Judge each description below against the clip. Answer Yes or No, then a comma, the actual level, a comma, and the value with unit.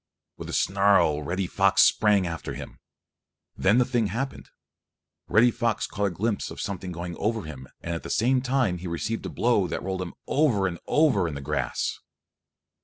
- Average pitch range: Yes, average, 4.8 semitones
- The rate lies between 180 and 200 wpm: Yes, average, 185 wpm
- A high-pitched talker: No, low, 100 Hz